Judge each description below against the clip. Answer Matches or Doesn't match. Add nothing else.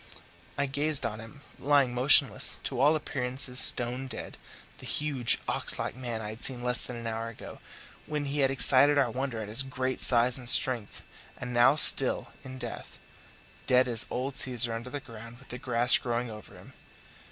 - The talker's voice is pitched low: Matches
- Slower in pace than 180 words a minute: Doesn't match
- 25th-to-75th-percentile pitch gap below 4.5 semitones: Matches